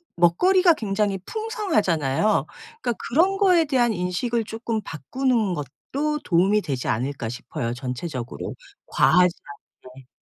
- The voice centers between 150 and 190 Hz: No, high, 200 Hz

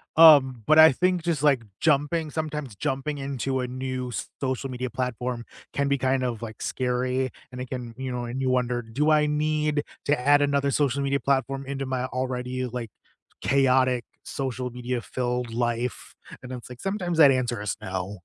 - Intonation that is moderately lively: No, narrow, 2.2 semitones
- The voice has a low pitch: Yes, low, 130 Hz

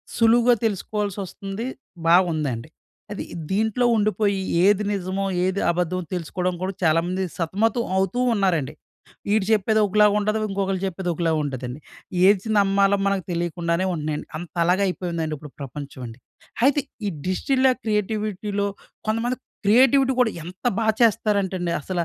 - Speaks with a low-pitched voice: No, high, 195 Hz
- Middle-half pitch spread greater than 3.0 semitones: Yes, average, 3.6 semitones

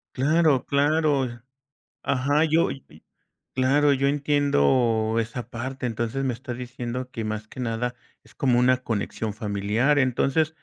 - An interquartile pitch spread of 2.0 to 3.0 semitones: No, average, 3.4 semitones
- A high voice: No, low, 130 Hz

